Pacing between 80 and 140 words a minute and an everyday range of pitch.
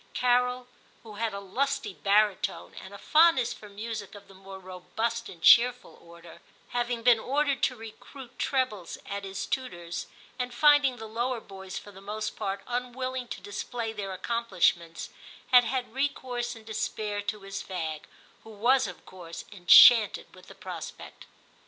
No: average, 160 wpm; average, 4.1 semitones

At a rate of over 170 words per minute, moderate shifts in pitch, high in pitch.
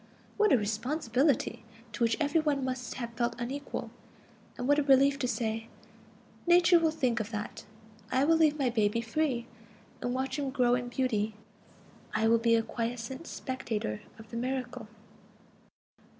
No: average, 160 wpm; average, 3.4 semitones; very high, 250 Hz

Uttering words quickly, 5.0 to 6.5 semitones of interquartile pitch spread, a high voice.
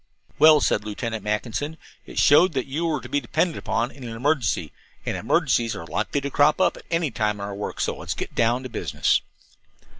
No: fast, 210 wpm; average, 5.3 semitones; low, 125 Hz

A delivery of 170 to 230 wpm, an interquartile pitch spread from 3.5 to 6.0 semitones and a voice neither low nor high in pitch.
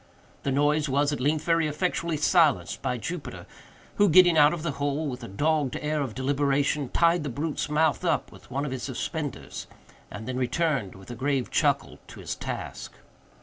No: average, 190 wpm; average, 3.0 semitones; medium, 145 Hz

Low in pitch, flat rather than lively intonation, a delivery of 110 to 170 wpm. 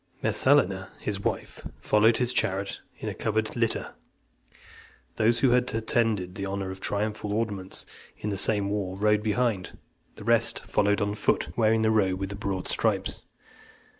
Yes: low, 105 Hz; narrow, 2.1 semitones; average, 160 wpm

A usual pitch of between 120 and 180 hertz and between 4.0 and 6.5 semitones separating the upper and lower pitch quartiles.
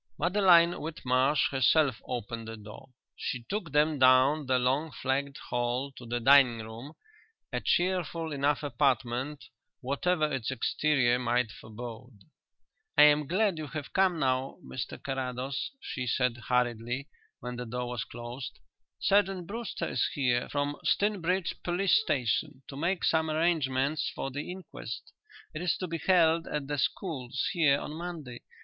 Yes: medium, 140 Hz; average, 4.5 semitones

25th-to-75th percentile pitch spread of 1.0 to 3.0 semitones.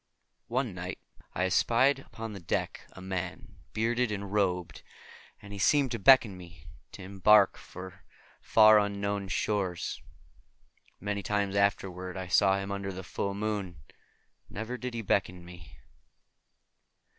Yes: narrow, 2.5 semitones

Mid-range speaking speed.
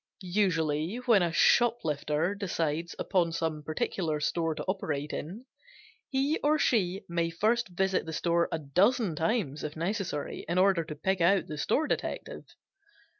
Yes: average, 150 wpm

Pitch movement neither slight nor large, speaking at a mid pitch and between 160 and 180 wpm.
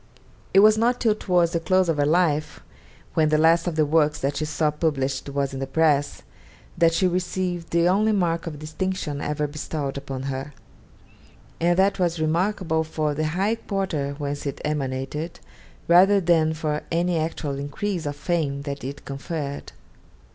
Yes: average, 3.4 semitones; medium, 160 Hz; average, 170 wpm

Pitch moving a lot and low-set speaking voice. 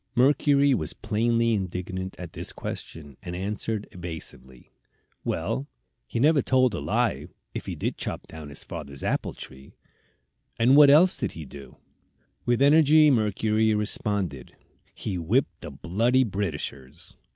Yes: wide, 7.3 semitones; low, 105 Hz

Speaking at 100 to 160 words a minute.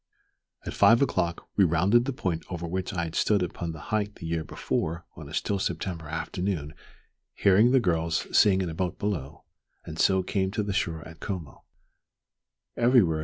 No: average, 175 wpm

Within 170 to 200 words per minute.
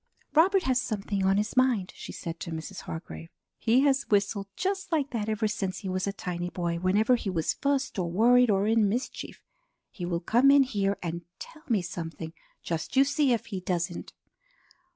Yes: average, 195 wpm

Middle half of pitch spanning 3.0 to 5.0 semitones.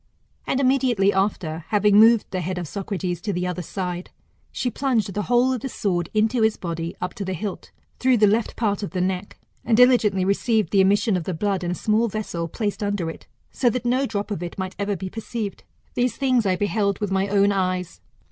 Yes: average, 3.3 semitones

